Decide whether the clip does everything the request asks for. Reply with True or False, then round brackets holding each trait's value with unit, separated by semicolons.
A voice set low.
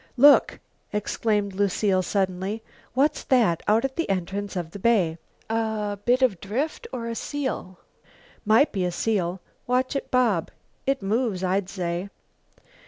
False (210 Hz)